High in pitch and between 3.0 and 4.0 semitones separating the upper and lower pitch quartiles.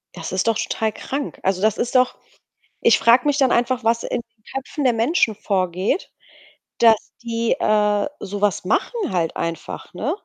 Yes: high, 225 Hz; average, 3.6 semitones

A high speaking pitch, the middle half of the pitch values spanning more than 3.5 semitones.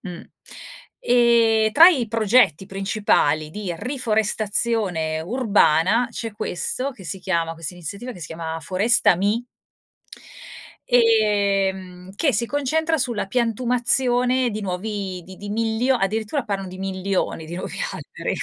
Yes: high, 210 Hz; average, 4.3 semitones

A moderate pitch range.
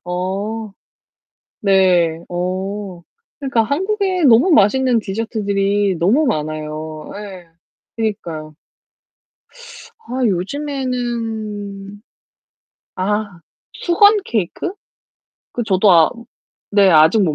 Yes: average, 4.6 semitones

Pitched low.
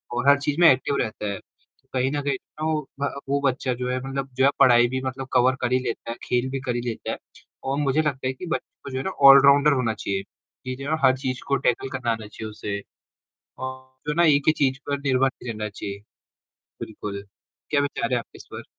Yes: low, 130 Hz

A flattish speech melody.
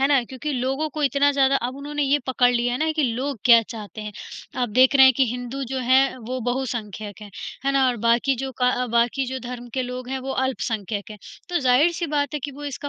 Yes: narrow, 2.3 semitones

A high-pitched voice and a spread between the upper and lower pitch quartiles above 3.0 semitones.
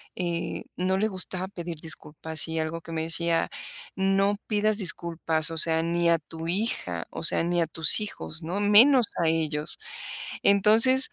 No: medium, 170 Hz; average, 3.6 semitones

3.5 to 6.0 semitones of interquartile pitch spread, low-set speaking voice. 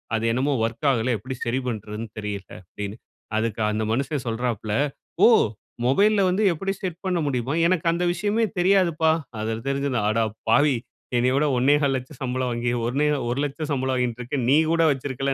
Yes: average, 4.6 semitones; low, 130 Hz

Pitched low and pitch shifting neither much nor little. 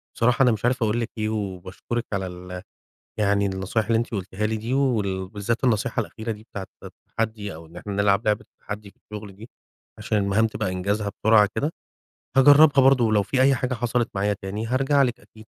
Yes: low, 110 Hz; average, 3.1 semitones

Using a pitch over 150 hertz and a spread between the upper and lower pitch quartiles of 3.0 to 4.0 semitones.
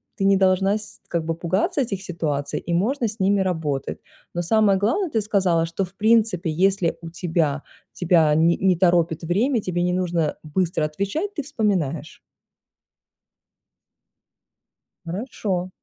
Yes: medium, 185 Hz; average, 3.5 semitones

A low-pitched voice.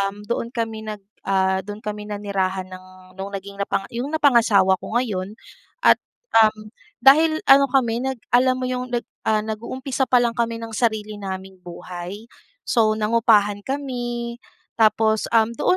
No: high, 220 Hz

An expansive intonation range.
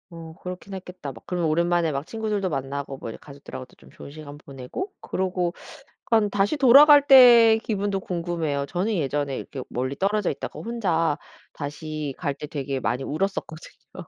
Yes: wide, 5.9 semitones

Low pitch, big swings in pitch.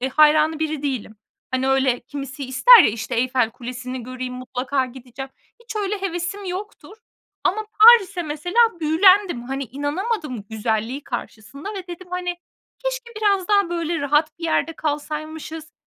No: very high, 300 Hz; wide, 6.1 semitones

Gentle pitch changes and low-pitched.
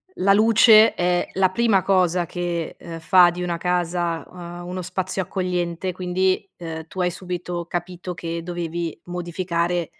No: narrow, 1.3 semitones; medium, 180 Hz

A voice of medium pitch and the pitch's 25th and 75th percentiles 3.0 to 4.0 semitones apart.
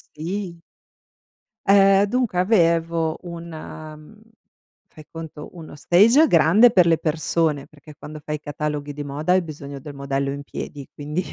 Yes: medium, 160 Hz; average, 3.3 semitones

